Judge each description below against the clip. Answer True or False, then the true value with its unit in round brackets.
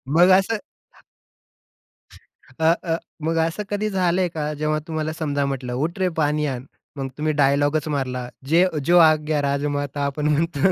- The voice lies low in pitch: False (155 Hz)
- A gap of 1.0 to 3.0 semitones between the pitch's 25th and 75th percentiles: True (2.7 semitones)